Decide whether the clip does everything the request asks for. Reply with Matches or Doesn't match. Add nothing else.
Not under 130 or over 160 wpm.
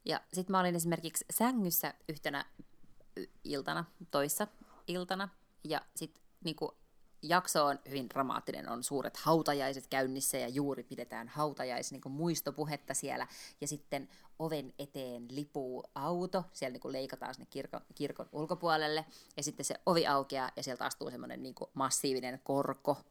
Matches